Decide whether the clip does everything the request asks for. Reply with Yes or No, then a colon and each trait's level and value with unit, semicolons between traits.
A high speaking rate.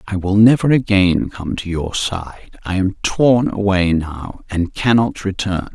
No: average, 165 wpm